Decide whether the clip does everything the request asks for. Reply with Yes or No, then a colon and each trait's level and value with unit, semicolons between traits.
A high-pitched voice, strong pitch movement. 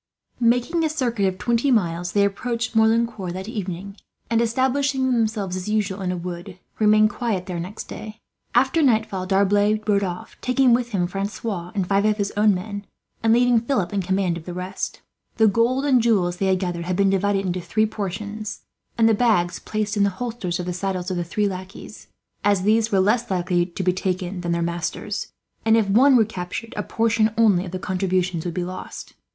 No: high, 200 Hz; average, 3.7 semitones